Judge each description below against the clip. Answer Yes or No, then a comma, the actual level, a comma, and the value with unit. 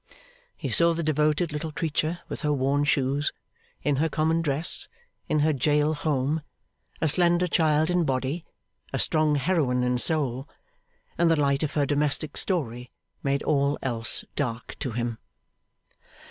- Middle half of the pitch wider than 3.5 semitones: No, average, 2.7 semitones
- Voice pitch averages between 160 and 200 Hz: No, medium, 150 Hz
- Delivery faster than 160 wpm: No, average, 150 wpm